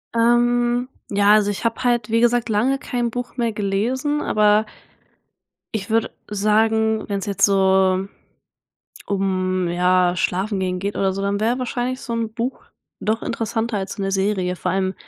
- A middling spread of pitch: Yes, average, 3.3 semitones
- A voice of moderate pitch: No, high, 210 Hz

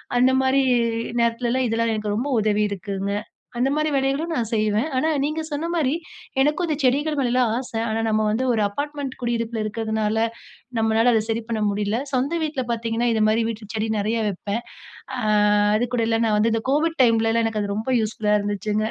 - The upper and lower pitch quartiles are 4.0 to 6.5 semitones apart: No, average, 3.3 semitones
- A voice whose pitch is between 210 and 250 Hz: Yes, high, 230 Hz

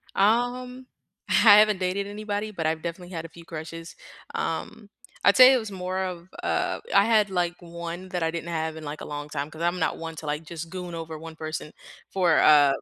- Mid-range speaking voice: Yes, medium, 170 Hz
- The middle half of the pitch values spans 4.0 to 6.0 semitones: No, average, 3.6 semitones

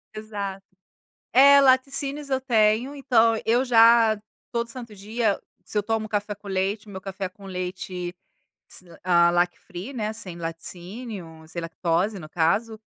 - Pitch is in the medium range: No, high, 210 Hz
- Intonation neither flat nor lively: Yes, average, 4.2 semitones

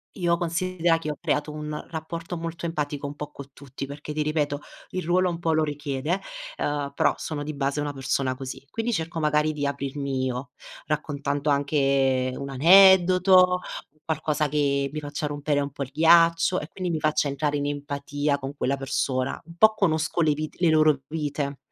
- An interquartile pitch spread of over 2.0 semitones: Yes, narrow, 2.6 semitones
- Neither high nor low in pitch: Yes, medium, 150 Hz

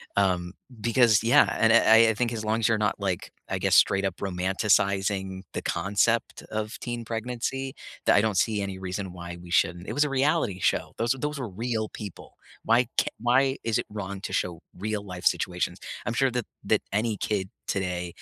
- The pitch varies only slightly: No, average, 3.4 semitones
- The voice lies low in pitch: Yes, low, 105 Hz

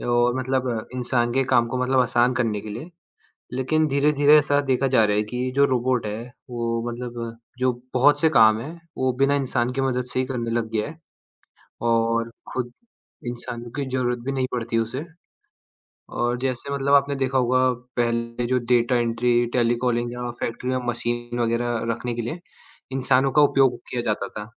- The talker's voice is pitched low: Yes, low, 125 Hz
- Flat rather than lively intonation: Yes, narrow, 1.9 semitones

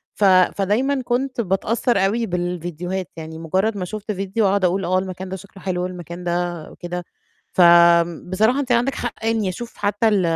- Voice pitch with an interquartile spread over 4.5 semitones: No, average, 3.5 semitones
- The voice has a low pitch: No, high, 190 Hz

